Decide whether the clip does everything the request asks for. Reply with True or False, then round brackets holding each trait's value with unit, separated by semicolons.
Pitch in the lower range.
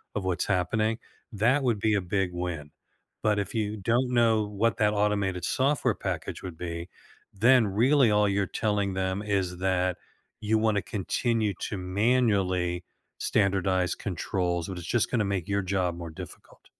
True (100 Hz)